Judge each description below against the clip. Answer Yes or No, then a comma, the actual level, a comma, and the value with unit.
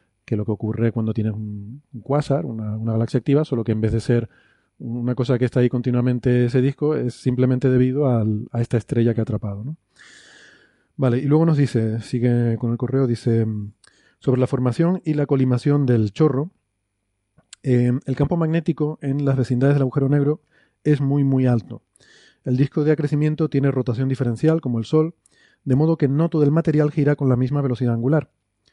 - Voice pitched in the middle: No, low, 130 Hz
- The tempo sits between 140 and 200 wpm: Yes, fast, 190 wpm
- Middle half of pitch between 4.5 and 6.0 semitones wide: No, average, 3.6 semitones